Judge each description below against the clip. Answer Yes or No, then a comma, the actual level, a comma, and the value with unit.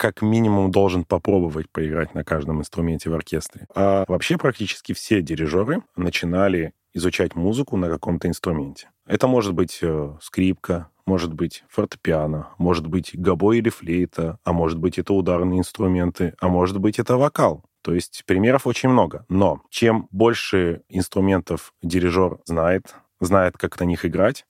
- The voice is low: Yes, very low, 90 Hz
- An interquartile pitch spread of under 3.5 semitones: Yes, average, 2.8 semitones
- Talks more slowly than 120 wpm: No, average, 145 wpm